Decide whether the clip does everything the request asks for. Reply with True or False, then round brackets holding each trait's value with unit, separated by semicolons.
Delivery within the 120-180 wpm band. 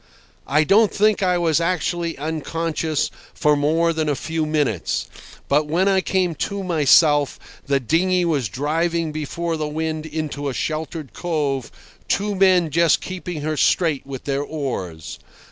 True (150 wpm)